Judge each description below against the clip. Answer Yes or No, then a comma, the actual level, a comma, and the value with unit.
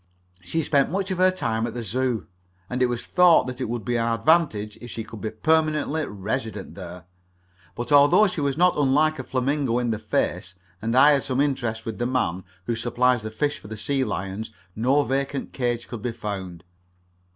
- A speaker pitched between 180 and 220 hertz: No, low, 125 Hz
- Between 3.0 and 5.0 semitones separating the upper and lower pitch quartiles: Yes, average, 4.5 semitones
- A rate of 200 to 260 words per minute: Yes, fast, 205 wpm